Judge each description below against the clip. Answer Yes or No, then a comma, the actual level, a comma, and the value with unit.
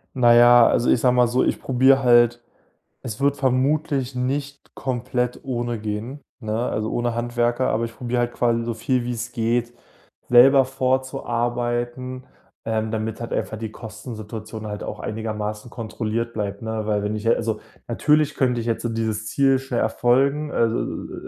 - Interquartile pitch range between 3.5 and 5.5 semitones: No, narrow, 2.4 semitones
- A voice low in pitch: Yes, low, 120 Hz